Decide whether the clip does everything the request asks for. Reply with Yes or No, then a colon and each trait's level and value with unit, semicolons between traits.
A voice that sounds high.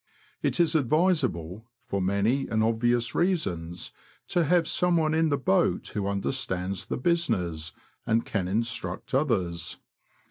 No: low, 115 Hz